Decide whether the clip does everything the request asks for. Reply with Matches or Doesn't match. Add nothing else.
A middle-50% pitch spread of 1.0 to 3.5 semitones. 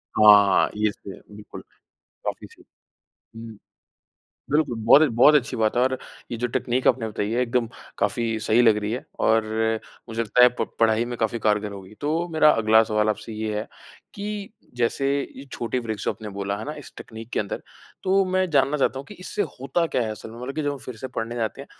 Doesn't match